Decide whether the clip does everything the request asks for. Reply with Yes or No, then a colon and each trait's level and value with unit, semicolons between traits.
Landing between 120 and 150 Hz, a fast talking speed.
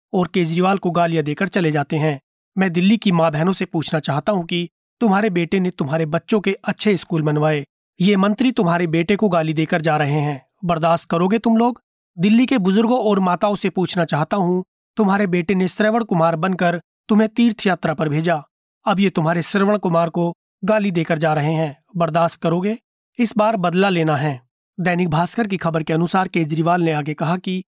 No: medium, 180 Hz; fast, 195 wpm